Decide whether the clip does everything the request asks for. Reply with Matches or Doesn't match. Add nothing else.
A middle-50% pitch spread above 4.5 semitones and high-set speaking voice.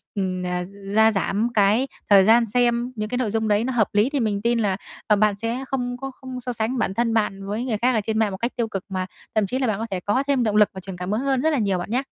Doesn't match